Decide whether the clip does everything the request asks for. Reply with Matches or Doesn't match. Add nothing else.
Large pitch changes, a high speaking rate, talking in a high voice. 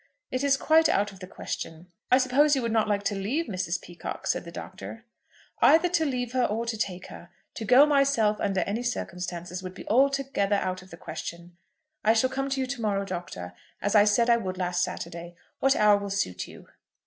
Matches